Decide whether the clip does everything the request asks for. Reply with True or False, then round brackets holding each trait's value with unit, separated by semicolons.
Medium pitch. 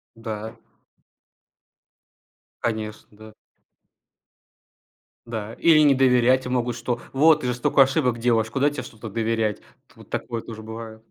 False (115 Hz)